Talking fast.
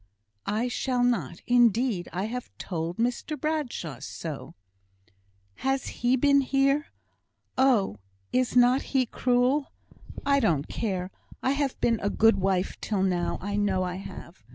No: slow, 135 wpm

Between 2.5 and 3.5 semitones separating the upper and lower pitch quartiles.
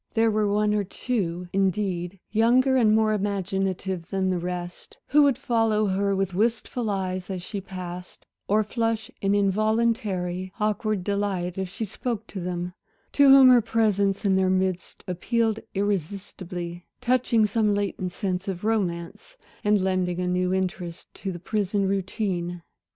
Yes: average, 3.0 semitones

